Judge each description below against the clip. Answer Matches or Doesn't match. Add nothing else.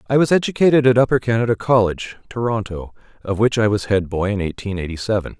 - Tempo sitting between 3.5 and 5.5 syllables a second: Doesn't match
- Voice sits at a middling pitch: Doesn't match